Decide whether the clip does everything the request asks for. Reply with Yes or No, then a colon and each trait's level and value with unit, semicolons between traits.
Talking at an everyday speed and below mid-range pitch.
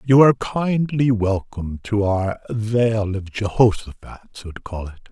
Yes: average, 150 wpm; low, 110 Hz